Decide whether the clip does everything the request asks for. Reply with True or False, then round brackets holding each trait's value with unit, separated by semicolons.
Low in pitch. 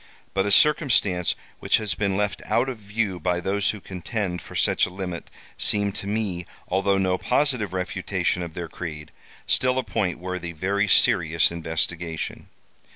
True (95 Hz)